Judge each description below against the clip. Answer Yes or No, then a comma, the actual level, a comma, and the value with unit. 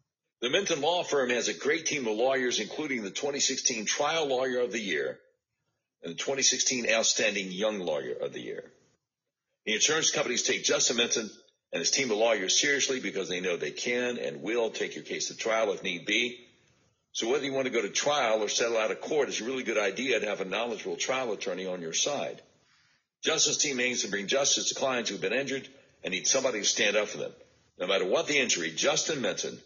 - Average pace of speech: No, fast, 220 wpm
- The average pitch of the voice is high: No, low, 135 Hz